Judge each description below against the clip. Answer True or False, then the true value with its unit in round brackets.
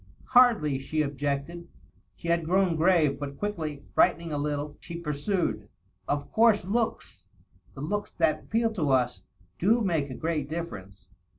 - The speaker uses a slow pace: False (160 wpm)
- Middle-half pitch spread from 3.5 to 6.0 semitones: True (4.7 semitones)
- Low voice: False (155 Hz)